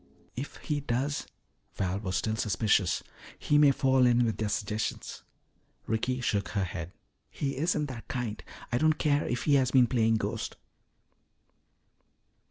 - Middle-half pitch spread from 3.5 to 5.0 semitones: Yes, average, 4.5 semitones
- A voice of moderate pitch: No, low, 120 Hz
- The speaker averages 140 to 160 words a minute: Yes, average, 155 wpm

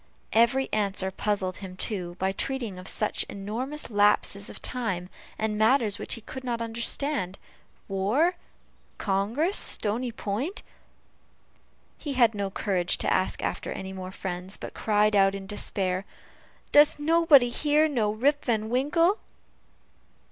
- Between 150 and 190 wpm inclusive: No, average, 140 wpm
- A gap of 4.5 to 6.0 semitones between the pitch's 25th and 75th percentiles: Yes, average, 5.3 semitones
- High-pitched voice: Yes, high, 215 Hz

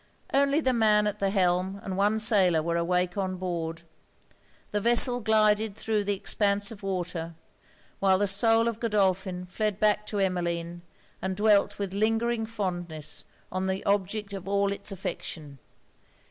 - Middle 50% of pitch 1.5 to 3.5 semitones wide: Yes, average, 2.8 semitones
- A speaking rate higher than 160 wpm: No, average, 155 wpm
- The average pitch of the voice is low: No, high, 200 Hz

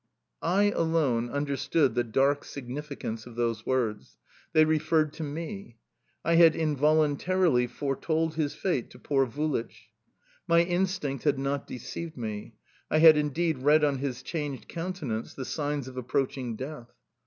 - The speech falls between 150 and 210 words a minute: No, average, 140 wpm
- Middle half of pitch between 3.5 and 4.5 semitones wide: Yes, average, 3.9 semitones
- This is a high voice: No, medium, 145 Hz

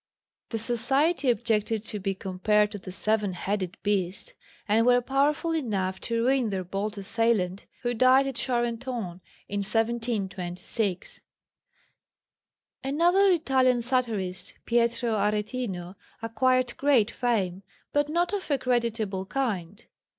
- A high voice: Yes, high, 230 Hz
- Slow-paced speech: Yes, slow, 120 wpm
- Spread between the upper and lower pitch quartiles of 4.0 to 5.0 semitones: Yes, average, 4.3 semitones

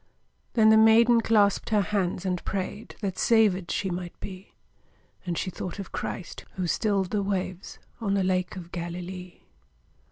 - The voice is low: No, high, 190 Hz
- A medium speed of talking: Yes, average, 160 wpm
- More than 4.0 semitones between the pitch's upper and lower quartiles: No, narrow, 2.4 semitones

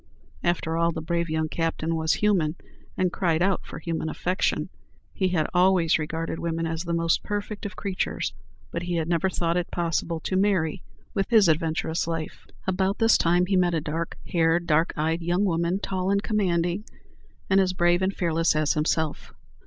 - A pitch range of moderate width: No, narrow, 2.3 semitones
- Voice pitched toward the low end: No, medium, 170 Hz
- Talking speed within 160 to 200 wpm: Yes, average, 185 wpm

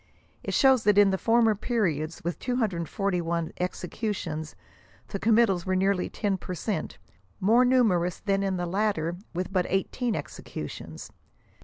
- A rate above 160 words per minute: No, average, 140 wpm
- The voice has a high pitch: Yes, high, 195 Hz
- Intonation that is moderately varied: Yes, average, 3.8 semitones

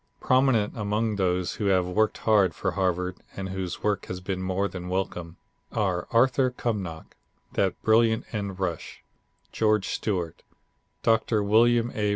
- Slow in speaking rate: No, average, 145 wpm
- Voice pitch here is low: Yes, low, 100 Hz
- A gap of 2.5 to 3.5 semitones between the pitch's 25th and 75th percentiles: Yes, average, 3.2 semitones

